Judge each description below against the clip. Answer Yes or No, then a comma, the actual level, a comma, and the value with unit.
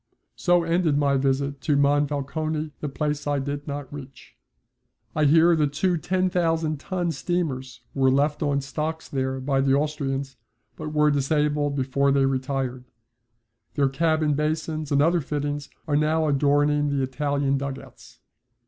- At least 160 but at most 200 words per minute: No, average, 150 wpm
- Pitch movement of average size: No, narrow, 2.0 semitones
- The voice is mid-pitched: Yes, medium, 145 Hz